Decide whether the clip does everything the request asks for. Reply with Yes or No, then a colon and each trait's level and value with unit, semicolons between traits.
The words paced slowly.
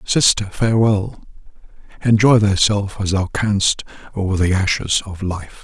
Yes: slow, 130 wpm